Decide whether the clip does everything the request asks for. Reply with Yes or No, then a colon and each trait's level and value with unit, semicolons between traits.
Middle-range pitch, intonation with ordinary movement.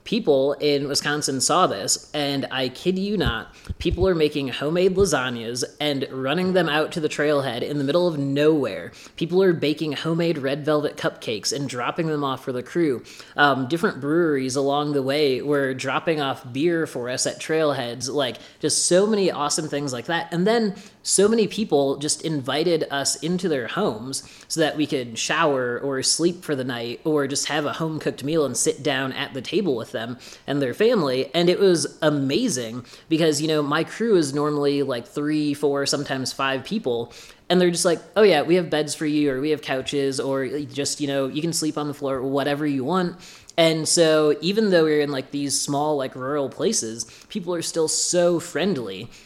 Yes: medium, 150 Hz; average, 3.1 semitones